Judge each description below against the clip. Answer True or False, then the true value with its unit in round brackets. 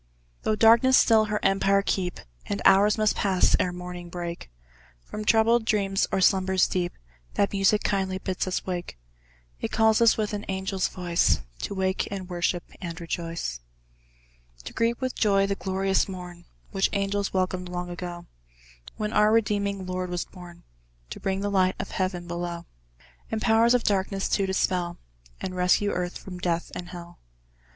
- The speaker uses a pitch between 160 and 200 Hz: True (190 Hz)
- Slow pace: False (165 wpm)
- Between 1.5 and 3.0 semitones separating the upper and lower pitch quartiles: True (2.4 semitones)